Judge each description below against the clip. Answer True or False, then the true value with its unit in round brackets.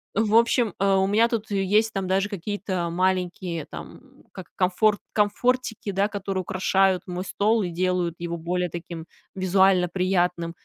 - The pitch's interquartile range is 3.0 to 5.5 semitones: False (2.5 semitones)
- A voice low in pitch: False (190 Hz)